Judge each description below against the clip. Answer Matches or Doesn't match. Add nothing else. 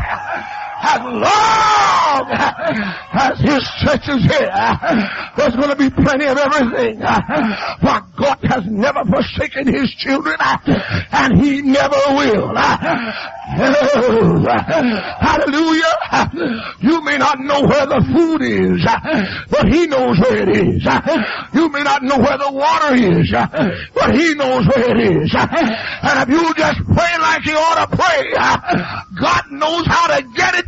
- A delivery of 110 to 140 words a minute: Matches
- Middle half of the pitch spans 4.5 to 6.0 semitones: Doesn't match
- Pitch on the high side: Matches